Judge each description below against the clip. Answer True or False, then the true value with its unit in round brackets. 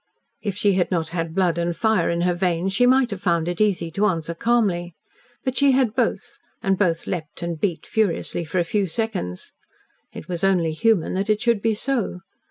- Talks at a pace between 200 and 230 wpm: True (205 wpm)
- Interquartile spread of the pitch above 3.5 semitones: True (4.2 semitones)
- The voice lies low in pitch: False (185 Hz)